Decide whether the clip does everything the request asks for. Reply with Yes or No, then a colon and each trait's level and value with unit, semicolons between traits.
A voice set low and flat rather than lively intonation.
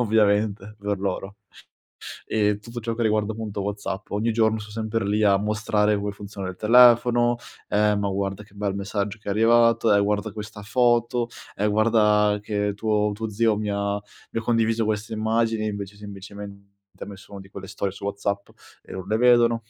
Yes: low, 105 Hz; narrow, 1.7 semitones